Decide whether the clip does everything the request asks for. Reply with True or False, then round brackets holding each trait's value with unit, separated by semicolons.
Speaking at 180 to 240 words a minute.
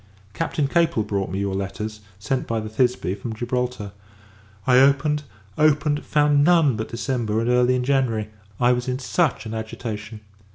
False (165 wpm)